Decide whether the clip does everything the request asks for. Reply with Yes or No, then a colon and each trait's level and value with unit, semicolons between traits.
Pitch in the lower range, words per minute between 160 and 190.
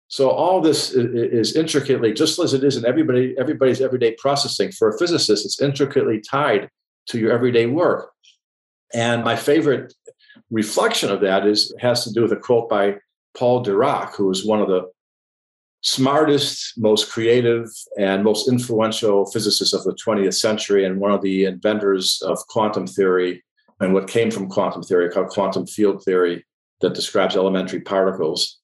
Yes: low, 115 Hz; average, 165 wpm